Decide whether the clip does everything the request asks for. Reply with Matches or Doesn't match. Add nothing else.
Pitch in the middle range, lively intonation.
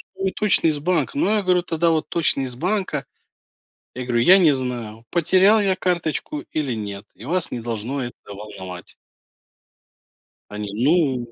Matches